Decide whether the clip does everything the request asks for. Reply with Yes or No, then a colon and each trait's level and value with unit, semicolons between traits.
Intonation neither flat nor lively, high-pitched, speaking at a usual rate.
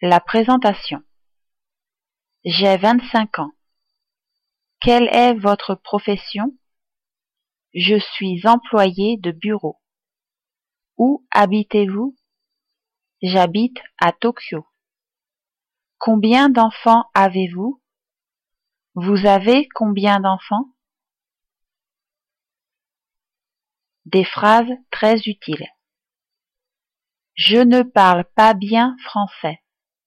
No: average, 3.7 semitones; high, 215 Hz; slow, 70 wpm